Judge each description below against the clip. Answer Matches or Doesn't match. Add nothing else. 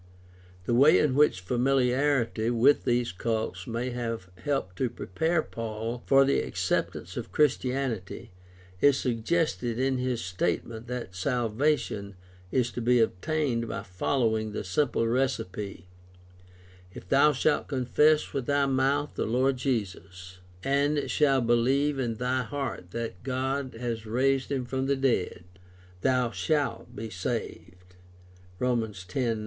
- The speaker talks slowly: Matches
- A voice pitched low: Matches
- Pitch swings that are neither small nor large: Matches